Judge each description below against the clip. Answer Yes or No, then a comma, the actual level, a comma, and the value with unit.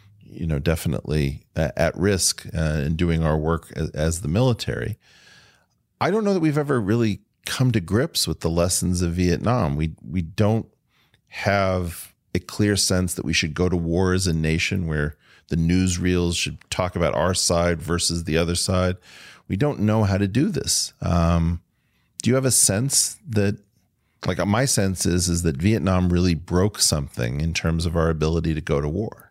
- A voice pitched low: Yes, very low, 90 Hz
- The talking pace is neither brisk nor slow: Yes, average, 185 wpm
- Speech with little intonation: No, average, 3.9 semitones